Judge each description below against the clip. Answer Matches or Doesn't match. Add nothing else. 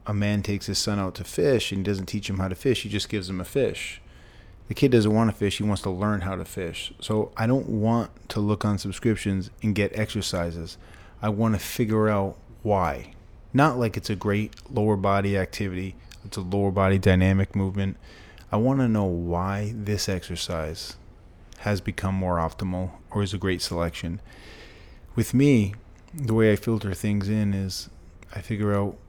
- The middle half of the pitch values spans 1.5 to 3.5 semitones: Matches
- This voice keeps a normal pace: Matches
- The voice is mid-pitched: Doesn't match